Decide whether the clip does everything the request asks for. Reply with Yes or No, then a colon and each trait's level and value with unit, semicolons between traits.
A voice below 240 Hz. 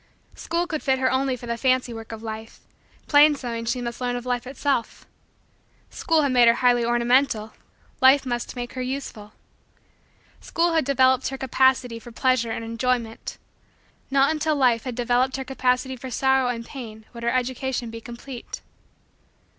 No: very high, 250 Hz